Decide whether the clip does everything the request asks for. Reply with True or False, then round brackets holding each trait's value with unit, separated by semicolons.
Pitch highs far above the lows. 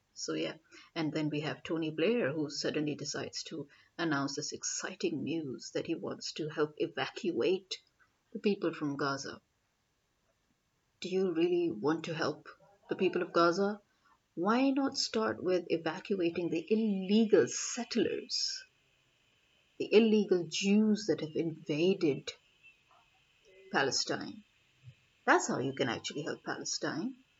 True (6.3 semitones)